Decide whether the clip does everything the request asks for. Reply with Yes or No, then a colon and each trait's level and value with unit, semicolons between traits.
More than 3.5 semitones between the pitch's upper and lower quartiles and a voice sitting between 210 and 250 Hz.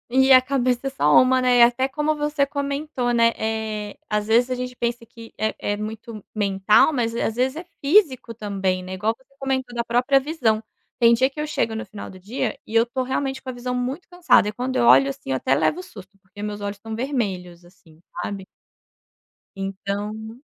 Yes: average, 4.1 semitones; high, 235 Hz